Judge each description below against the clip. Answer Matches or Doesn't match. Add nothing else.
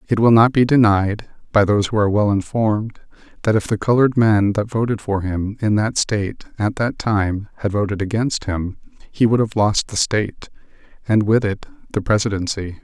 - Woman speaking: Doesn't match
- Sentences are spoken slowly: Doesn't match